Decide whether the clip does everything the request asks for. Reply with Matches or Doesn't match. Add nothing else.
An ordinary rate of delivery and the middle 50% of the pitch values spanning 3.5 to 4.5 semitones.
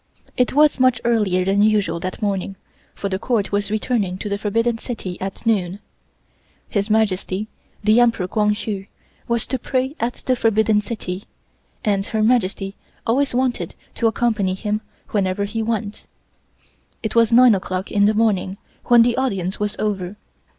Doesn't match